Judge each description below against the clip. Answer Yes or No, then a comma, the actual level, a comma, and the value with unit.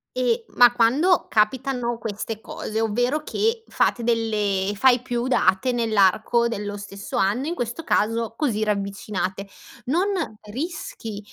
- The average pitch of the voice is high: Yes, high, 230 Hz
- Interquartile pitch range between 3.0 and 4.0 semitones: Yes, average, 3.4 semitones